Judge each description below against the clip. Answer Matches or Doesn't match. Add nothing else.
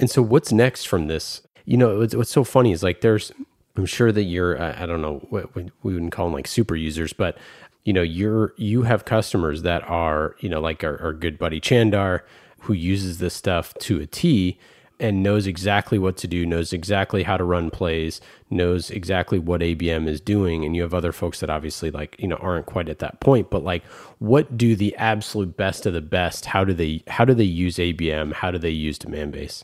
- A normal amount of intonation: Matches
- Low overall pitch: Matches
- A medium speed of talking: Doesn't match